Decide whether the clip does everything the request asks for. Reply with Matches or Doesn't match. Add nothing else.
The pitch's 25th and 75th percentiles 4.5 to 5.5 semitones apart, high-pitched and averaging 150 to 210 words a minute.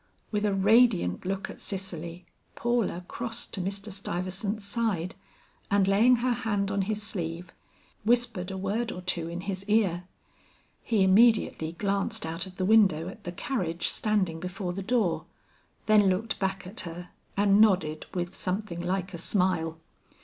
Doesn't match